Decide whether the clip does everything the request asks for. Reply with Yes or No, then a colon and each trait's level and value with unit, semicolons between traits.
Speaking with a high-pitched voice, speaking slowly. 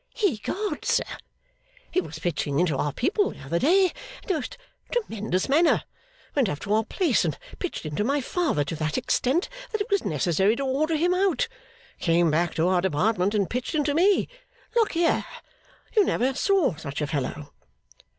No: very high, 250 Hz; average, 180 wpm